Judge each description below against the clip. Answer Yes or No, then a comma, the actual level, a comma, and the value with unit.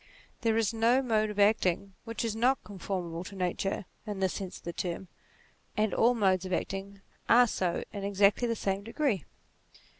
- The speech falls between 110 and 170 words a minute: No, average, 190 wpm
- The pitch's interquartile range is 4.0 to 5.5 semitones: No, average, 3.1 semitones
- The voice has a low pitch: No, high, 200 Hz